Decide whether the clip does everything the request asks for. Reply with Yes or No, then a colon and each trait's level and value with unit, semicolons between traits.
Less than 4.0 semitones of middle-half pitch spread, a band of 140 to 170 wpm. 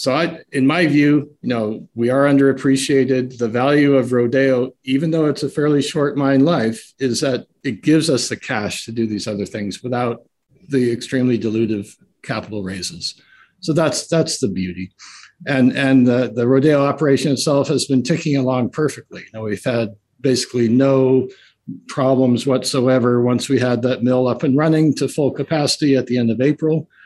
No: average, 2.8 semitones; average, 180 wpm